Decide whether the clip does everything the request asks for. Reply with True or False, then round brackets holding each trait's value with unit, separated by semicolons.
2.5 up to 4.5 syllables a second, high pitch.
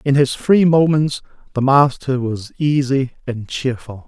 False (4.1 syllables/s; 135 Hz)